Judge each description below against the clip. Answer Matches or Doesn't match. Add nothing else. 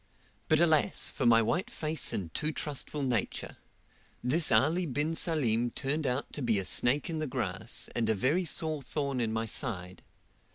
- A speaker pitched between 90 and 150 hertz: Matches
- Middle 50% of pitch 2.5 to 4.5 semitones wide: Doesn't match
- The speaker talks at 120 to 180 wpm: Matches